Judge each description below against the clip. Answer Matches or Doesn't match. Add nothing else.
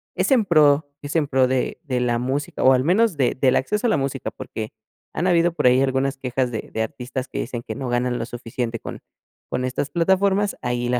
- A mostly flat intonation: Doesn't match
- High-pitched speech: Doesn't match